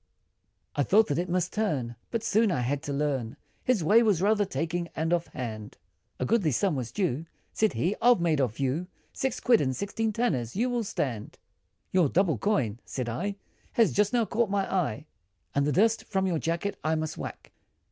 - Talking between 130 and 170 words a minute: No, average, 200 wpm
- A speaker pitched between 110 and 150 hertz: No, medium, 175 Hz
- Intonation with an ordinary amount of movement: No, wide, 6.9 semitones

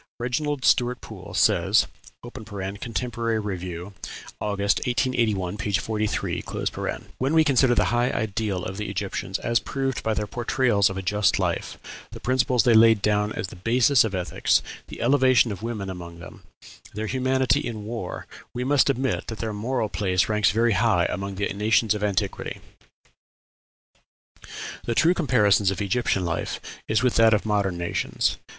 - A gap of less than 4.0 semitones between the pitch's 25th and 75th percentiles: Yes, average, 3.5 semitones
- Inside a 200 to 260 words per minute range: No, average, 155 wpm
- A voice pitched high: No, low, 110 Hz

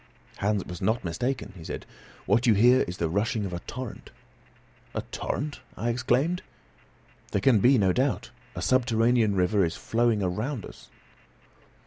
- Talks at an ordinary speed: Yes, average, 155 wpm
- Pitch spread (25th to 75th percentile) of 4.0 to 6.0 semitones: Yes, average, 4.5 semitones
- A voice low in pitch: Yes, low, 115 Hz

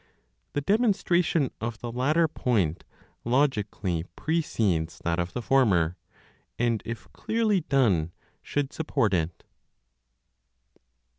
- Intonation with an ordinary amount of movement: No, wide, 8.6 semitones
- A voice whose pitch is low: Yes, low, 120 Hz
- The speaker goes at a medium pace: No, slow, 100 wpm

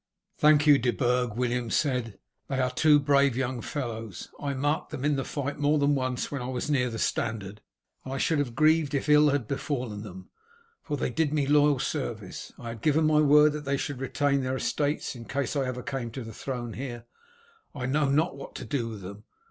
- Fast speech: Yes, fast, 220 wpm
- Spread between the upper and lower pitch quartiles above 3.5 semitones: No, average, 3.1 semitones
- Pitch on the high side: No, low, 135 Hz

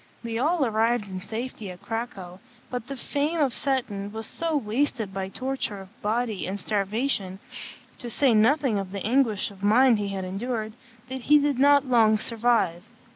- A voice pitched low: No, high, 225 Hz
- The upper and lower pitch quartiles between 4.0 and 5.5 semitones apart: Yes, average, 4.5 semitones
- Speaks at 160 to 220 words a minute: Yes, average, 175 wpm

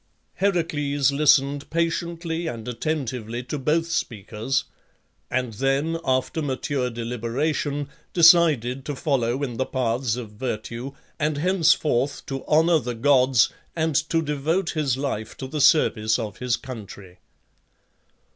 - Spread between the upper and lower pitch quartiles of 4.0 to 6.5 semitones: Yes, average, 4.3 semitones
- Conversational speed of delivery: No, slow, 125 wpm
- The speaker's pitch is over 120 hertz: Yes, low, 135 Hz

